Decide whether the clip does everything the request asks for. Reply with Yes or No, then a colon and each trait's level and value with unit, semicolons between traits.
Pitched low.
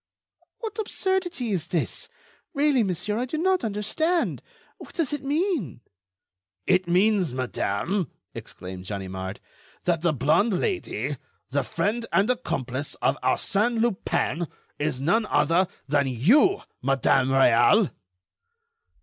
No: high, 190 Hz